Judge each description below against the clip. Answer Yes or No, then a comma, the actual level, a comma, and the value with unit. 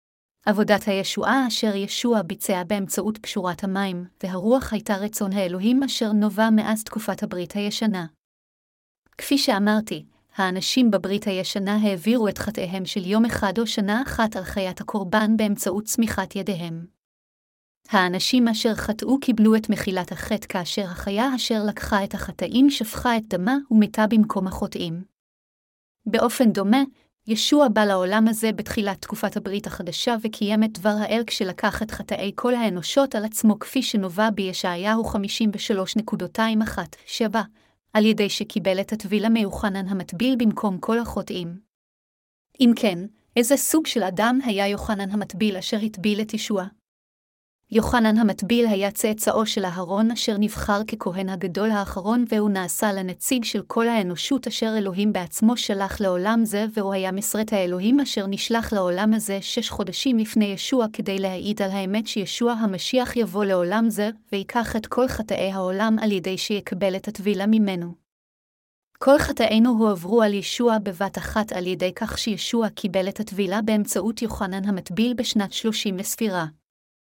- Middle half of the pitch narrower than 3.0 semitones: Yes, narrow, 2.5 semitones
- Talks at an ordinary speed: Yes, average, 140 wpm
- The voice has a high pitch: Yes, high, 210 Hz